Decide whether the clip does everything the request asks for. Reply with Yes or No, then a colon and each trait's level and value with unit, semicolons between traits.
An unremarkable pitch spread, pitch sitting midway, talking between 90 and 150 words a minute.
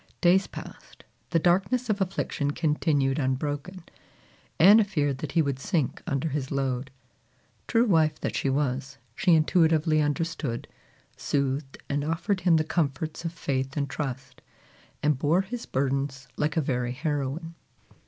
Yes: average, 3.7 semitones; medium, 150 Hz; average, 145 wpm